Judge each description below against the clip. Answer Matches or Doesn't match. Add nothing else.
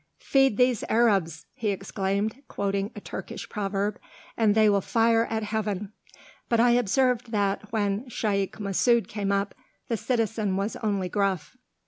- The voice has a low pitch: Doesn't match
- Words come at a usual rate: Matches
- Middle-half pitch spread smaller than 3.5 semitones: Matches